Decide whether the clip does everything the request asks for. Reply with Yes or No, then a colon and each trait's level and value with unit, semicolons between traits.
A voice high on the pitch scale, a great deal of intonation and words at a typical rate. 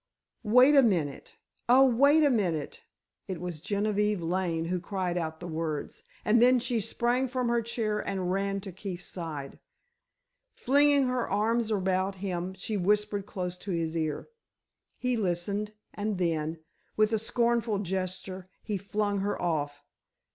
No: high, 200 Hz; average, 4.3 semitones; average, 150 wpm